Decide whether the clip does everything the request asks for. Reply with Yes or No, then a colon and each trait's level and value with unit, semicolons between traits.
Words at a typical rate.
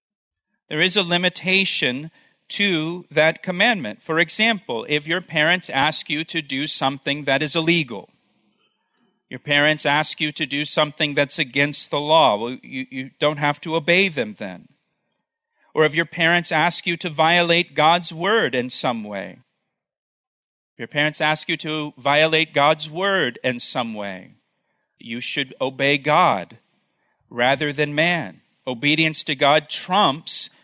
Yes: average, 150 wpm